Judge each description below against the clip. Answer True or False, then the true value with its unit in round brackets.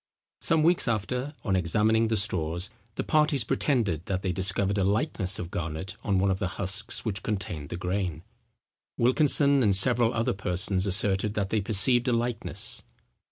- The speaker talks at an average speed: True (165 wpm)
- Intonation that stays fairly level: False (3.8 semitones)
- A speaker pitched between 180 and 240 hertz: False (100 Hz)